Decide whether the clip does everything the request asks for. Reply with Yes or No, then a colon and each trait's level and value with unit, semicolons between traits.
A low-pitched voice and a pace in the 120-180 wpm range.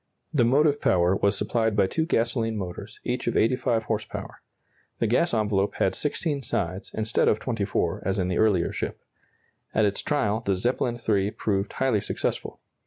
Yes: low, 110 Hz; average, 175 wpm